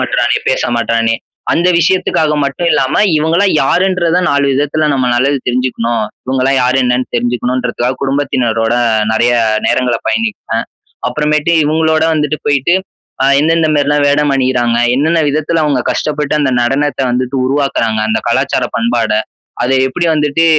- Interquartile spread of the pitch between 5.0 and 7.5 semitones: No, average, 3.6 semitones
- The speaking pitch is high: No, medium, 140 Hz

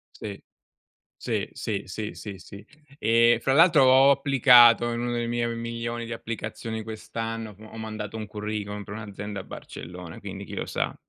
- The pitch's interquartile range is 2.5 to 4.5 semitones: No, narrow, 2.1 semitones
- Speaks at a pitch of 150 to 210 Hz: No, low, 115 Hz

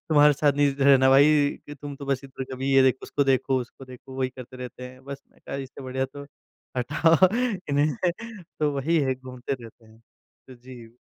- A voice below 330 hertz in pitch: Yes, low, 135 Hz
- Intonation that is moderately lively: No, narrow, 1.8 semitones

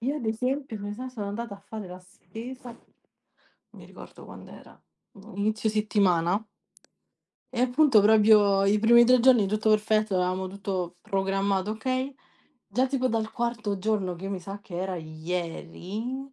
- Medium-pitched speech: No, high, 210 Hz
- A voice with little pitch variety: No, average, 3.5 semitones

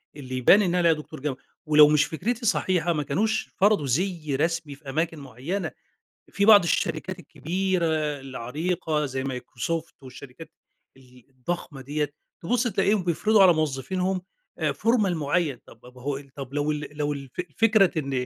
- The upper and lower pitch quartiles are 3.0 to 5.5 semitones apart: Yes, average, 5.2 semitones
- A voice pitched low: No, medium, 155 Hz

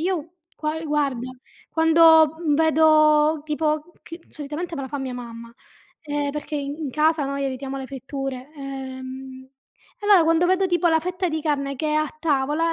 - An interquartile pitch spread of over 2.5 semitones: Yes, average, 2.9 semitones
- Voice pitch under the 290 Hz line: No, very high, 300 Hz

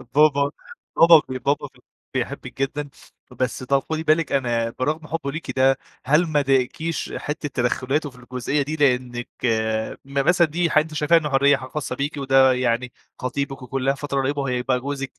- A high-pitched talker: No, medium, 140 Hz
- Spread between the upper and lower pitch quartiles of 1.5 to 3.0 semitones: Yes, average, 2.7 semitones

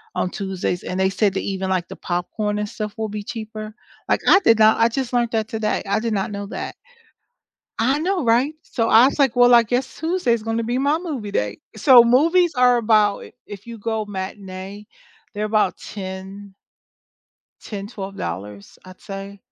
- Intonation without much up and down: No, average, 3.5 semitones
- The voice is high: Yes, high, 215 Hz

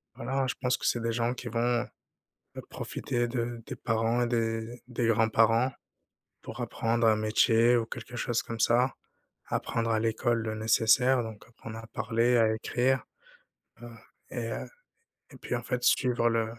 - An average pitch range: No, narrow, 1.4 semitones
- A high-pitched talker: No, low, 115 Hz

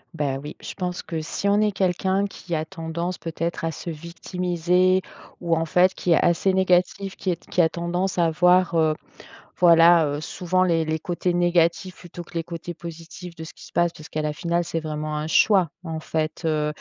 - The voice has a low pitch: No, medium, 170 Hz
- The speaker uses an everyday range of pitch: No, narrow, 1.9 semitones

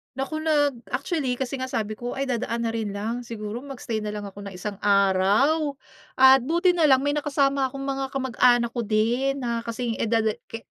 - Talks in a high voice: Yes, high, 245 Hz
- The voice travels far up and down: No, average, 3.6 semitones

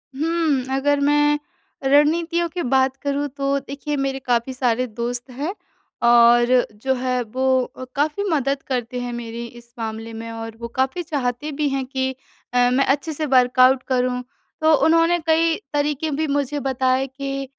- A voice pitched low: No, very high, 270 Hz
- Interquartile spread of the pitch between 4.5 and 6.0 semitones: No, average, 2.9 semitones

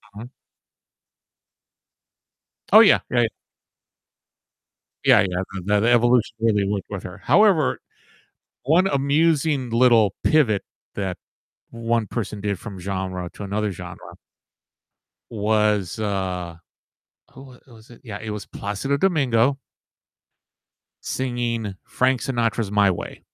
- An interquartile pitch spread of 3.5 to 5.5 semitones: Yes, average, 3.9 semitones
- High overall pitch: No, low, 110 Hz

